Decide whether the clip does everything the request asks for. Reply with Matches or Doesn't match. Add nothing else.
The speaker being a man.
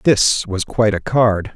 Matches